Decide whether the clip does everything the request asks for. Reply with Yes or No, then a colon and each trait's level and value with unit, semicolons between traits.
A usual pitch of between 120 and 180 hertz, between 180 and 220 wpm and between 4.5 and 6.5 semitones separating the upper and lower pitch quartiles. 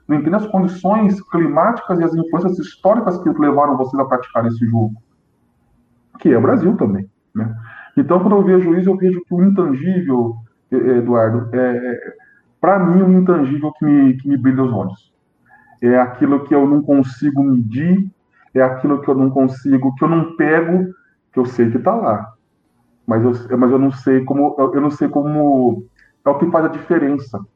Yes: medium, 140 Hz; fast, 185 wpm; average, 5.2 semitones